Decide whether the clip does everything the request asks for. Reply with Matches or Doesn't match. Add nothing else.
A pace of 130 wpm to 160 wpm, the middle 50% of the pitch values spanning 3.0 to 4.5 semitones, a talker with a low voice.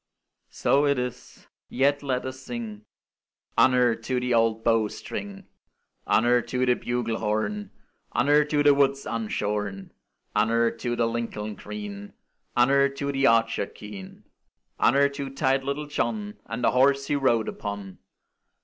Matches